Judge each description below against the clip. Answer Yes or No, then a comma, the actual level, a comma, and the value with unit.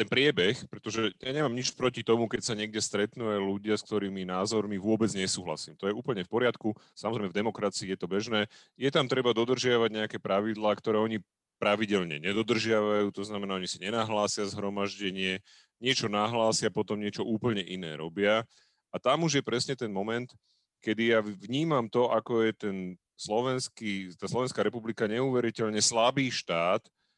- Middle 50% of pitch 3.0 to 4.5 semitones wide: No, narrow, 2.5 semitones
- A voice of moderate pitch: No, low, 110 Hz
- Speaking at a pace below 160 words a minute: No, fast, 165 wpm